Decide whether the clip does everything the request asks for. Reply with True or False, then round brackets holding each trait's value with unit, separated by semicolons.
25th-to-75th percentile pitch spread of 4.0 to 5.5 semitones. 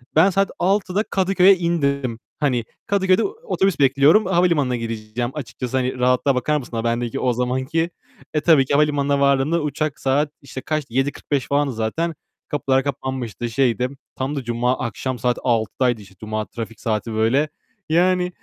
True (4.3 semitones)